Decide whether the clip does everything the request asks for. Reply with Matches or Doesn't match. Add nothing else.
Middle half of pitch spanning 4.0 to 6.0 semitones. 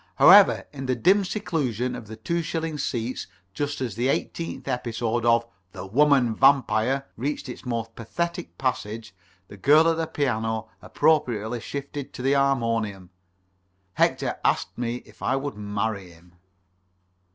Matches